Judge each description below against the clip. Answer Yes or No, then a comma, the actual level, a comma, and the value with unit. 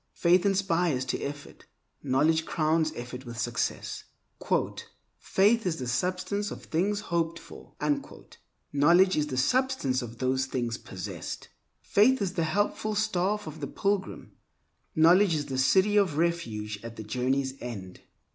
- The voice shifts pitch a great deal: Yes, wide, 6.8 semitones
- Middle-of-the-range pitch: Yes, medium, 160 Hz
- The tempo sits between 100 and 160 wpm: Yes, average, 140 wpm